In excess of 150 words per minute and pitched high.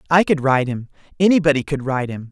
No: fast, 205 wpm; medium, 145 Hz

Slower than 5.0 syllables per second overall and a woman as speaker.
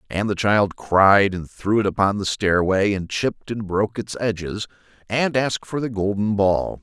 No: 4.7 syllables/s; male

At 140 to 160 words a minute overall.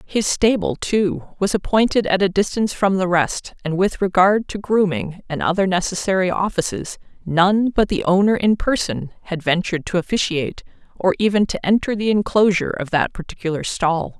No: average, 170 wpm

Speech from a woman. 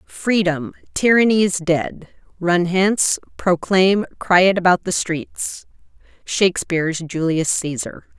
Yes: female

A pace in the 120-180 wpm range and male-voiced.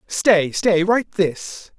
Yes: slow, 135 wpm; male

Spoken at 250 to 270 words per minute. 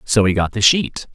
Yes: fast, 260 wpm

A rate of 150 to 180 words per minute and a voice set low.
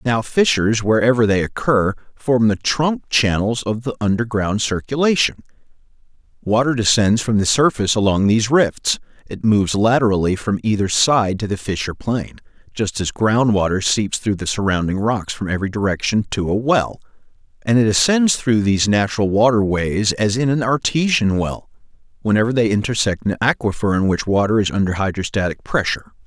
Yes: average, 160 wpm; low, 110 Hz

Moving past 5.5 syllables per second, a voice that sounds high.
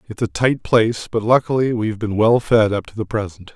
No: 5.7 syllables/s; low, 110 Hz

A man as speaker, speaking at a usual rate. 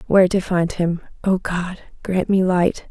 No: female; average, 165 wpm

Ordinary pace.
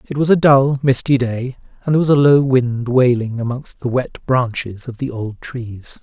No: fast, 210 wpm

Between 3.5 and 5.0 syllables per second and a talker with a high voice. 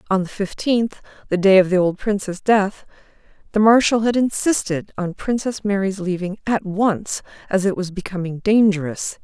Yes: 4.8 syllables/s; high, 195 Hz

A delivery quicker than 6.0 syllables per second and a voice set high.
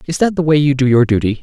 No: 7.0 syllables/s; medium, 140 Hz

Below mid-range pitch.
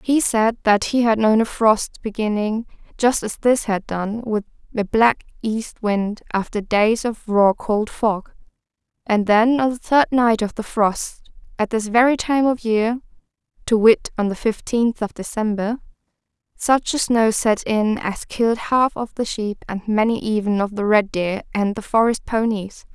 No: high, 220 Hz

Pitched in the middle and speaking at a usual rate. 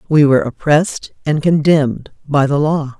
Yes: medium, 145 Hz; average, 160 wpm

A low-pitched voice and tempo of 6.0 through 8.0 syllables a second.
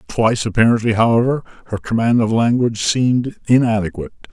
Yes: low, 115 Hz; 6.4 syllables/s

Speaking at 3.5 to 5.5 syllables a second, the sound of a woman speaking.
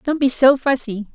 Yes: 5.1 syllables/s; female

